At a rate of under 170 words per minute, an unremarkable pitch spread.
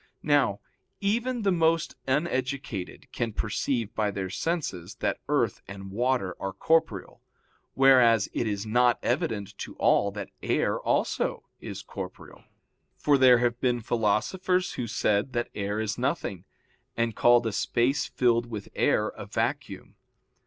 Yes: average, 145 wpm; average, 4.6 semitones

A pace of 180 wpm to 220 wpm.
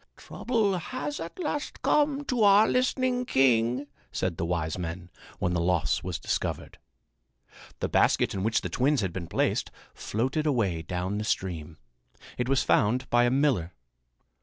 No: average, 160 wpm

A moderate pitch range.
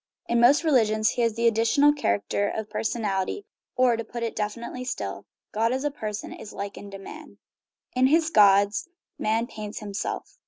Yes: average, 3.3 semitones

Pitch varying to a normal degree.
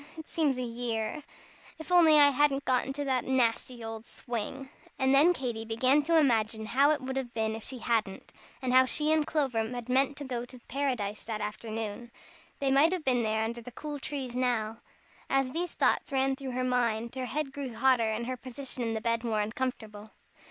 Yes: average, 3.3 semitones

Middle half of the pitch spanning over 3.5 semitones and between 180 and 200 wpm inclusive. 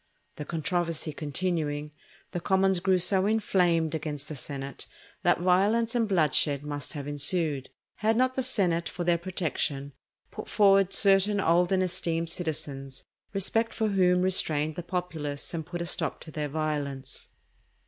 No: average, 4.3 semitones; average, 150 wpm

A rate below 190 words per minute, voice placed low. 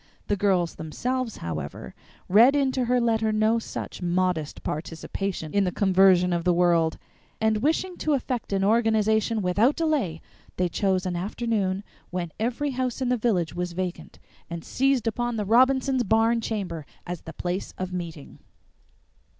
No: average, 155 wpm; high, 205 Hz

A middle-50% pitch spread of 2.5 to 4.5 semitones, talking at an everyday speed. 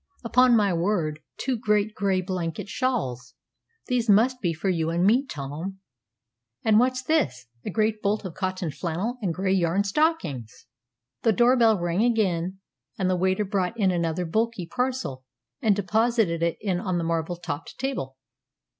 No: average, 5.1 semitones; average, 165 wpm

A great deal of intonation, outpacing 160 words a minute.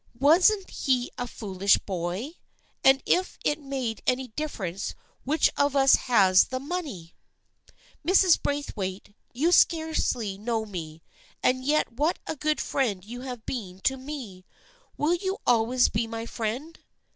No: wide, 5.9 semitones; average, 140 wpm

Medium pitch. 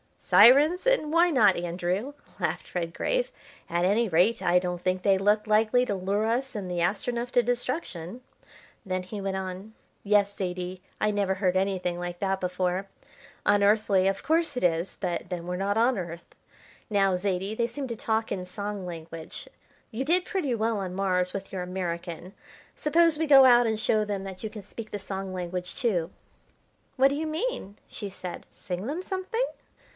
No: high, 200 Hz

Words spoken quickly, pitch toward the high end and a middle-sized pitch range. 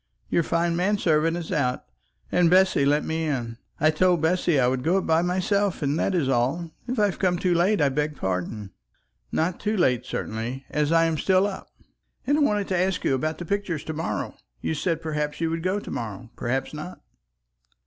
No: fast, 210 wpm; medium, 165 Hz; average, 4.4 semitones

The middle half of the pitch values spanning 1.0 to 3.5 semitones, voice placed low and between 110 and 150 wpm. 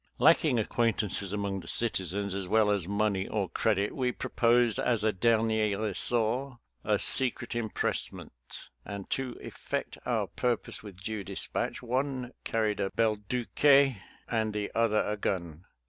Yes: average, 3.0 semitones; low, 110 Hz; average, 145 wpm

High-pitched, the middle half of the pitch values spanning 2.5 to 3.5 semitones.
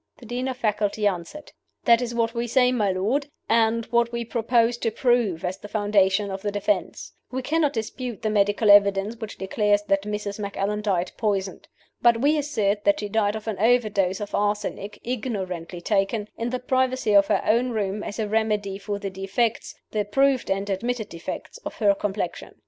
Yes: high, 210 Hz; average, 2.8 semitones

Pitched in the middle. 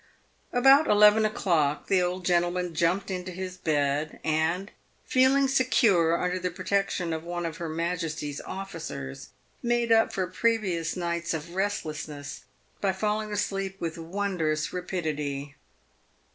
Yes: medium, 180 Hz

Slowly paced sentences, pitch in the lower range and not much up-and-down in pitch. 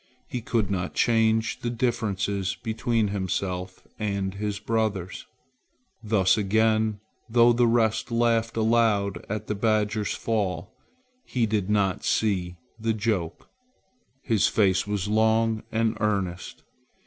Yes: slow, 120 wpm; low, 110 Hz; narrow, 2.3 semitones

